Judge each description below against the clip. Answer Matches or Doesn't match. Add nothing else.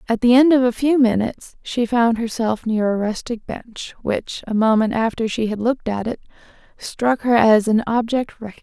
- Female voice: Matches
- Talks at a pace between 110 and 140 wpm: Doesn't match